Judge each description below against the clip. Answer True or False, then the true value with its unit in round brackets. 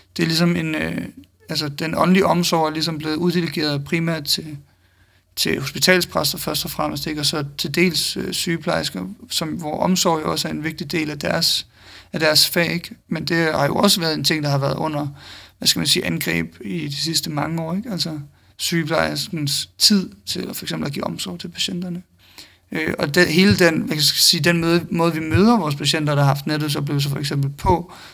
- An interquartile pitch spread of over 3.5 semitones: False (3.2 semitones)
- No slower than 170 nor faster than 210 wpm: False (220 wpm)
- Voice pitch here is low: False (160 Hz)